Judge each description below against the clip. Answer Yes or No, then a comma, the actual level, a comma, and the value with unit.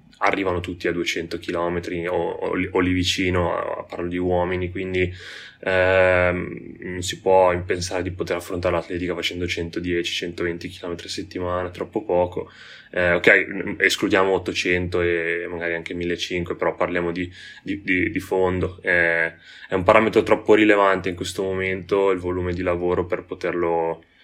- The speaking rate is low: No, average, 150 wpm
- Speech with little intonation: Yes, narrow, 1.0 semitones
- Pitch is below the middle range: Yes, very low, 90 Hz